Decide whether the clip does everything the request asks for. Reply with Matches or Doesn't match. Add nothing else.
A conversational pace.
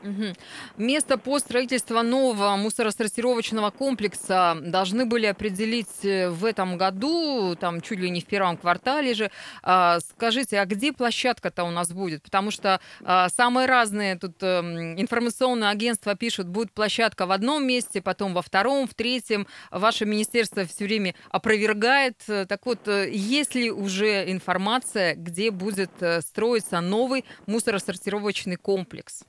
Matches